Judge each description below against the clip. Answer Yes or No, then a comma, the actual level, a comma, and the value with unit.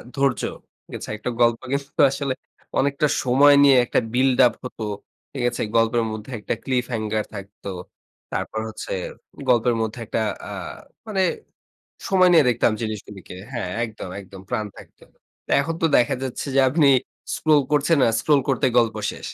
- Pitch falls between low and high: No, low, 125 Hz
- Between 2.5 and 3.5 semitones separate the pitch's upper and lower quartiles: No, average, 4.2 semitones